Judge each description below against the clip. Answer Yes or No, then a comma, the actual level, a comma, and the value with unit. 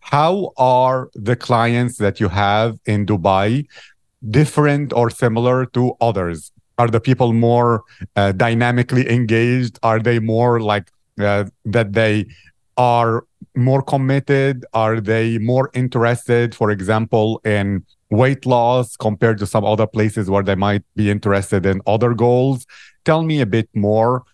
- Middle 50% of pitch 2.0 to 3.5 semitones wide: Yes, average, 2.7 semitones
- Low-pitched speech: Yes, low, 115 Hz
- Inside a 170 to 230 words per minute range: No, average, 145 wpm